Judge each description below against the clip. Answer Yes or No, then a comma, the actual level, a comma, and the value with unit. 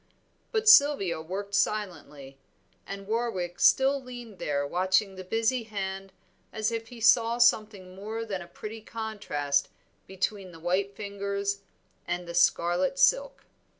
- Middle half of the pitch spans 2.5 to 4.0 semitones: Yes, average, 3.7 semitones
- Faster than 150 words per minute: No, slow, 135 wpm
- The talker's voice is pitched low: No, high, 200 Hz